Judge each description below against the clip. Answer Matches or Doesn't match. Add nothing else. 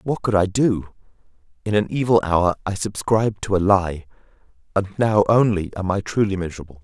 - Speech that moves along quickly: Doesn't match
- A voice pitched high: Doesn't match